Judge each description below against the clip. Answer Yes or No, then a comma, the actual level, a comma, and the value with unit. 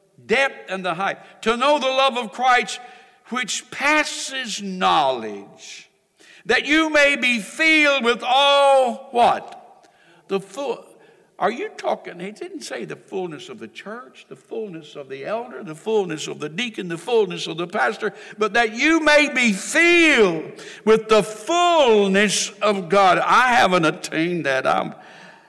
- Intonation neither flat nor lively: No, wide, 6.6 semitones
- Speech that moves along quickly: No, average, 155 wpm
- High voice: Yes, high, 235 Hz